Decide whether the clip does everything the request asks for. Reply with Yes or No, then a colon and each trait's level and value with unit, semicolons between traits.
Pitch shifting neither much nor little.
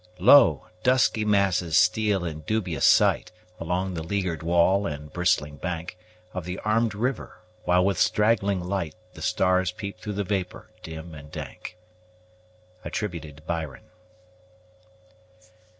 Yes: average, 3.6 semitones